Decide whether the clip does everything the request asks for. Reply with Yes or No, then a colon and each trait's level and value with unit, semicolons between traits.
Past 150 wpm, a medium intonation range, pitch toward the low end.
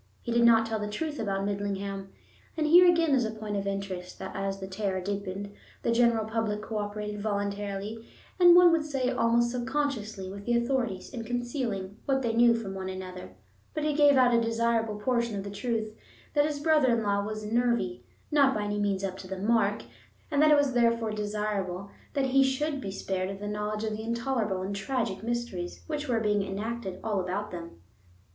No: average, 195 wpm; average, 3.6 semitones; high, 220 Hz